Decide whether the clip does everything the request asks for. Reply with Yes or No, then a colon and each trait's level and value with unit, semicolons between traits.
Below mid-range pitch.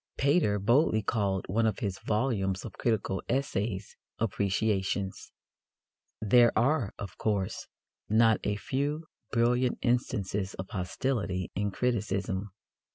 Yes: low, 105 Hz